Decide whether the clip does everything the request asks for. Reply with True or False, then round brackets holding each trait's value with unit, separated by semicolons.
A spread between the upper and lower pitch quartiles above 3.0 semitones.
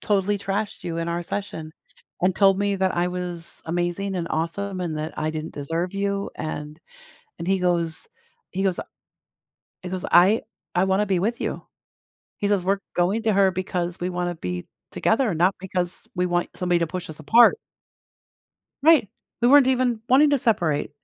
False (2.7 semitones)